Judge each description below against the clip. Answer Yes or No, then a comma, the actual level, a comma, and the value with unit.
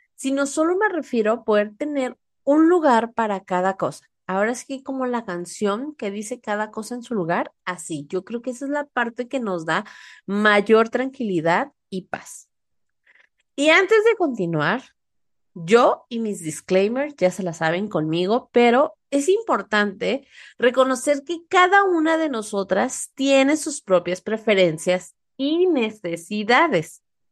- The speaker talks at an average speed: Yes, average, 150 wpm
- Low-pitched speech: No, high, 235 Hz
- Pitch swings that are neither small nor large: No, wide, 6.4 semitones